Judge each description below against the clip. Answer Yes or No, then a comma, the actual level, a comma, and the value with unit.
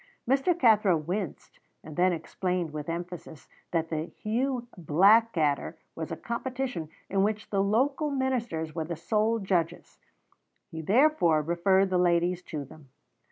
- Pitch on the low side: No, medium, 180 Hz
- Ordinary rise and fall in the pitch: No, wide, 5.8 semitones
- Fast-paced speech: No, average, 140 wpm